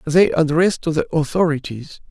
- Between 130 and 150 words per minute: Yes, average, 140 wpm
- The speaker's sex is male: Yes, male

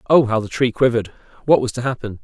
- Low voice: Yes, low, 120 Hz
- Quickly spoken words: Yes, fast, 240 wpm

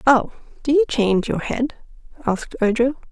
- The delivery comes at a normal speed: Yes, average, 155 wpm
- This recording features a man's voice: No, female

